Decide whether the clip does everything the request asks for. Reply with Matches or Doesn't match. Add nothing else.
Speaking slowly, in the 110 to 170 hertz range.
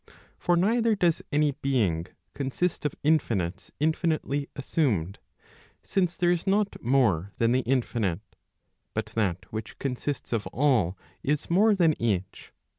Matches